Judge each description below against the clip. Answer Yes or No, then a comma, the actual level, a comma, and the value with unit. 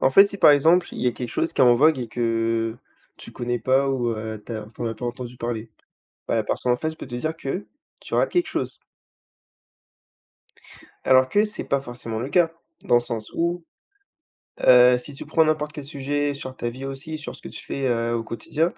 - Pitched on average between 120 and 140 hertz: Yes, low, 130 Hz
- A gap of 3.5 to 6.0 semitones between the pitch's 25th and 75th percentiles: Yes, average, 4.1 semitones